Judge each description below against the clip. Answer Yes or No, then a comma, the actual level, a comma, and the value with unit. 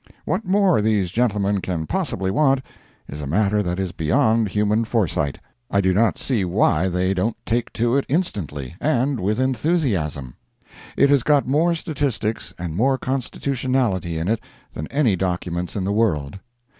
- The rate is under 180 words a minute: Yes, average, 160 wpm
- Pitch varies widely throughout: Yes, wide, 6.4 semitones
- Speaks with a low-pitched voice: Yes, low, 105 Hz